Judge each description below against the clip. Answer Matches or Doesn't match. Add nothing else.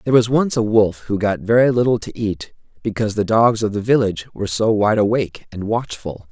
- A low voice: Matches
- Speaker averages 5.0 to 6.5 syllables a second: Matches